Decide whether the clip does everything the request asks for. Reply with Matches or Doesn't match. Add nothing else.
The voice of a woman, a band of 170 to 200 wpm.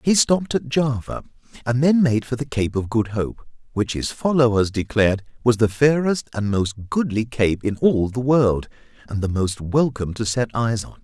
Doesn't match